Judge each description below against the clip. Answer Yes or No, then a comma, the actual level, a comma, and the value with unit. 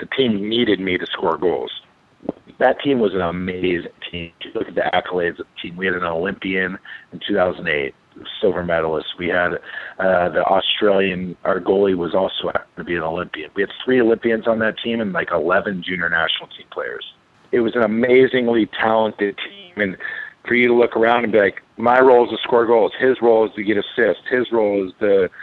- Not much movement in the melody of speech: No, average, 4.0 semitones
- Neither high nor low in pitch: No, low, 110 Hz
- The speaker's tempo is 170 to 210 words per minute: Yes, fast, 205 wpm